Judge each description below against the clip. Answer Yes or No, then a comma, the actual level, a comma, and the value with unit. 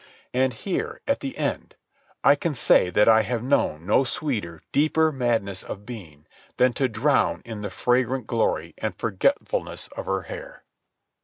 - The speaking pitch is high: No, low, 120 Hz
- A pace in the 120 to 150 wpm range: No, average, 160 wpm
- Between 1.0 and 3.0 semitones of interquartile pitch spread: No, average, 4.6 semitones